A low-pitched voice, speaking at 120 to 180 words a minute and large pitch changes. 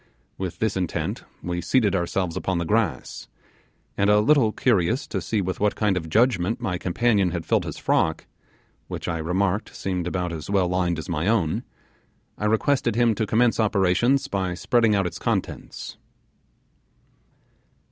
No: very low, 95 Hz; average, 160 wpm; average, 4.0 semitones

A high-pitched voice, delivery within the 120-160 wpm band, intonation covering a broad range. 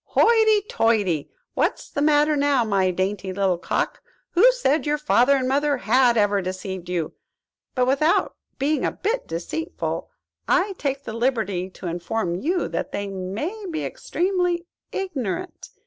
Yes: very high, 260 Hz; average, 150 wpm; wide, 8.7 semitones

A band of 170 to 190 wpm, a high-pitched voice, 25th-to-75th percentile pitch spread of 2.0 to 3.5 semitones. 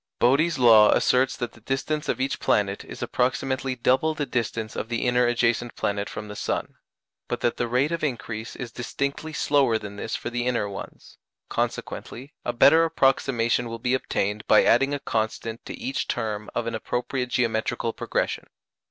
No: average, 180 wpm; low, 120 Hz; average, 3.0 semitones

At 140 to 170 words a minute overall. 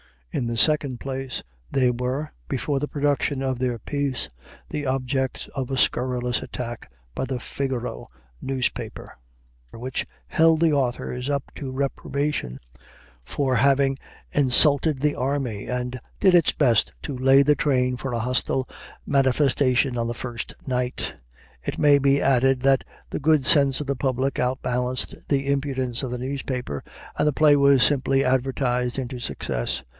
Yes: average, 150 wpm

